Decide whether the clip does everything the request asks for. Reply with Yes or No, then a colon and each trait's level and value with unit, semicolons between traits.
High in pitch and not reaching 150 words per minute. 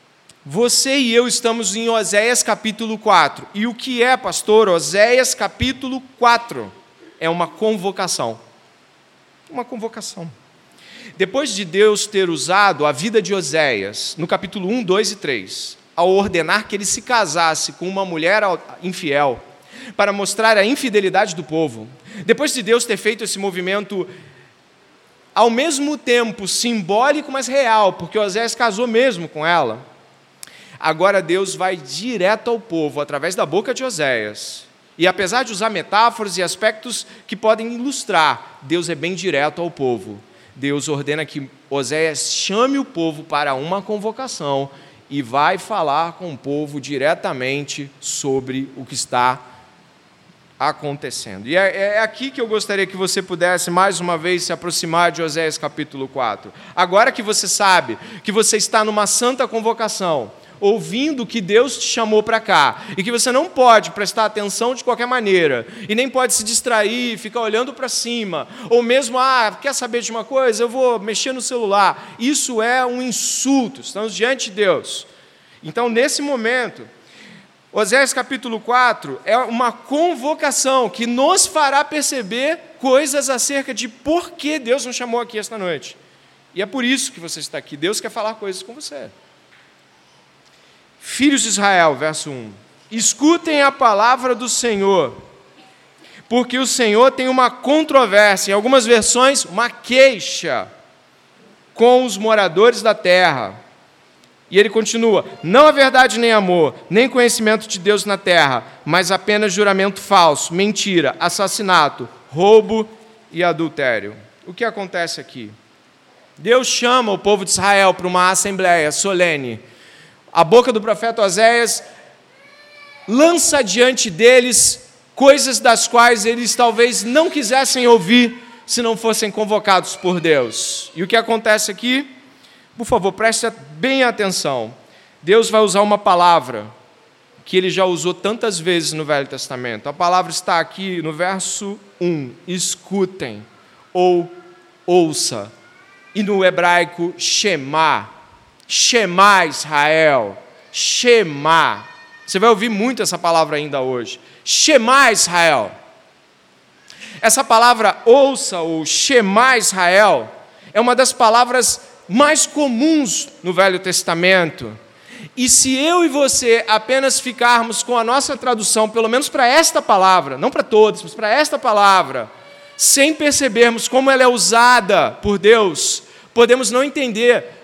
Yes: high, 215 Hz; average, 140 wpm